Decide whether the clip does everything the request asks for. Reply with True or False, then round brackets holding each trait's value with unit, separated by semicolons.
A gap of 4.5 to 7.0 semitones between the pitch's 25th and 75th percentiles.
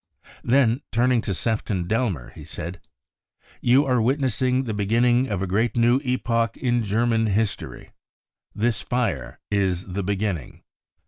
False (3.5 semitones)